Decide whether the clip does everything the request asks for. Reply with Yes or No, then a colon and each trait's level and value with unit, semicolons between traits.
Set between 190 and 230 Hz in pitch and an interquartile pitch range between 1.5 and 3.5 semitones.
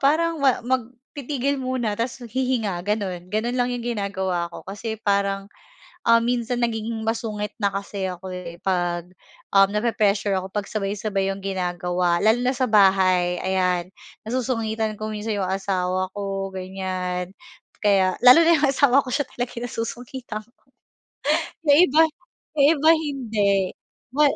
No: high, 215 Hz; average, 4.4 semitones